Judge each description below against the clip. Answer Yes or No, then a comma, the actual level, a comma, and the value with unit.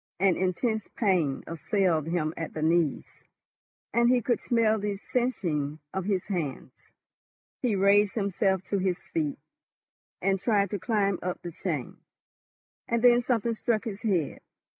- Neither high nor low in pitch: No, high, 195 Hz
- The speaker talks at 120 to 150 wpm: Yes, average, 145 wpm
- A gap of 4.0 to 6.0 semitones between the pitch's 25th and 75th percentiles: Yes, average, 4.4 semitones